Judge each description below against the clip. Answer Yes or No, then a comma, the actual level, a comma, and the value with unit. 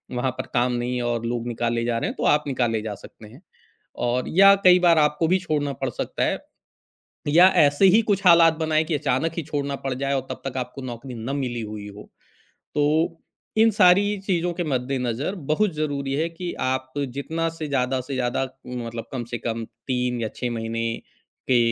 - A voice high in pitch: No, low, 135 Hz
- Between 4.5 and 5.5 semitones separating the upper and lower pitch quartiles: Yes, average, 4.8 semitones